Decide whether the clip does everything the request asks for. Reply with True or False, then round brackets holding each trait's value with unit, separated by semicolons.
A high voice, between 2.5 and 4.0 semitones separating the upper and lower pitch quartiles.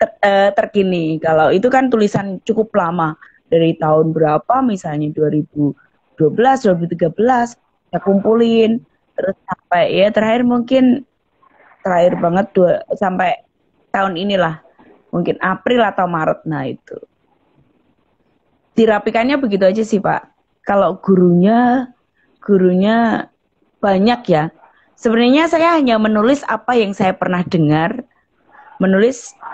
False (205 Hz; 5.4 semitones)